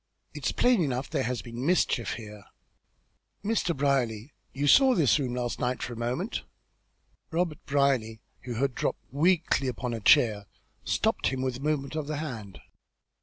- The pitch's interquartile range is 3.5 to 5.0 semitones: Yes, average, 4.2 semitones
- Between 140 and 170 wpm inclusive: Yes, average, 165 wpm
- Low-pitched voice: Yes, low, 130 Hz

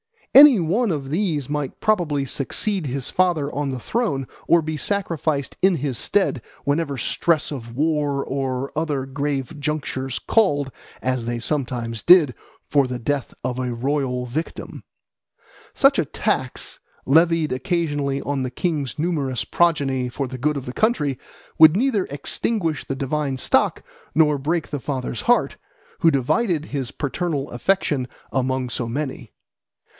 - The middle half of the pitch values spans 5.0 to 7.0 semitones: No, average, 3.7 semitones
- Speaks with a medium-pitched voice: Yes, medium, 145 Hz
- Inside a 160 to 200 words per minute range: No, average, 145 wpm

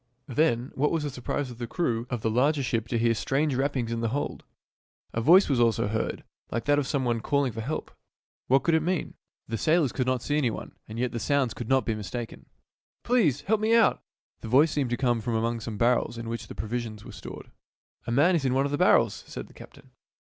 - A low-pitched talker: Yes, low, 125 Hz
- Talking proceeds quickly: Yes, fast, 250 wpm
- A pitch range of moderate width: Yes, average, 3.8 semitones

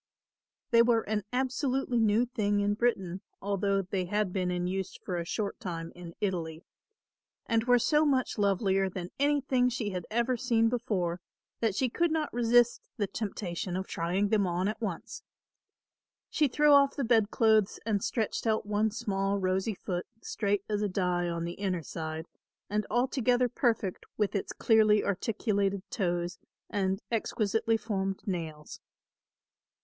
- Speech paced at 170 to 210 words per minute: No, average, 155 wpm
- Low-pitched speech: No, high, 205 Hz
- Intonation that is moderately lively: Yes, average, 3.8 semitones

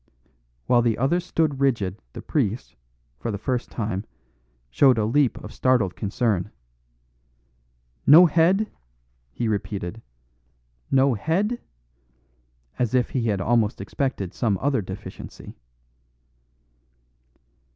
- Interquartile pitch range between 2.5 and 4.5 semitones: No, average, 5.1 semitones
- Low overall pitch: Yes, low, 120 Hz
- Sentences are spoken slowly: Yes, slow, 110 wpm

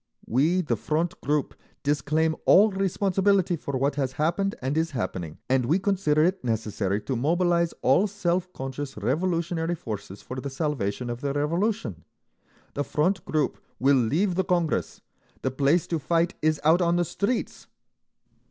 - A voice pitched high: No, medium, 155 Hz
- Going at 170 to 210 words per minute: No, average, 155 wpm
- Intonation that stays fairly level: No, average, 5.0 semitones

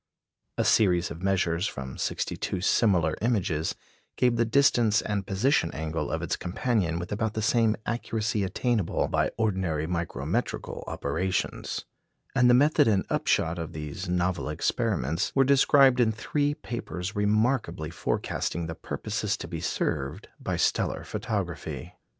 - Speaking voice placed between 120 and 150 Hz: No, low, 100 Hz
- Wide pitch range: Yes, wide, 5.7 semitones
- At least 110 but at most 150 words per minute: Yes, average, 140 wpm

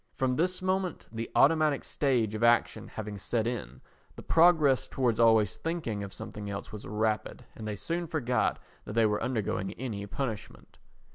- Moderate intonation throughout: No, wide, 5.7 semitones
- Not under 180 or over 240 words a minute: No, average, 165 wpm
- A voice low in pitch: Yes, low, 115 Hz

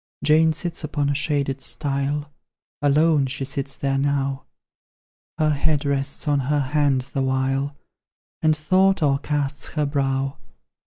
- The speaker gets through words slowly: Yes, slow, 130 wpm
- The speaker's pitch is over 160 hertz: No, medium, 140 Hz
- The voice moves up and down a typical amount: No, narrow, 1.8 semitones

